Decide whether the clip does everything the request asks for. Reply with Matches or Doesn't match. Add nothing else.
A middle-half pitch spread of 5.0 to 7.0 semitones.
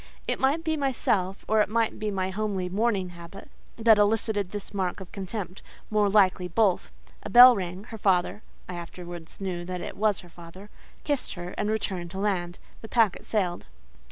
Doesn't match